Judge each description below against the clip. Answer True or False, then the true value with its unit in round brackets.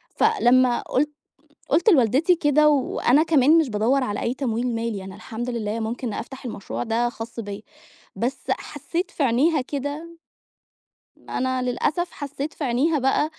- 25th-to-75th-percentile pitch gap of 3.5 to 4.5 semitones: True (4.2 semitones)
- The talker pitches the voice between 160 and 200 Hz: False (255 Hz)